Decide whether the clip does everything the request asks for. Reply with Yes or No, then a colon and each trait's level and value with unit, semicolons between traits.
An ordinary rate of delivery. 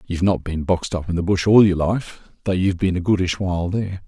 No: fast, 265 wpm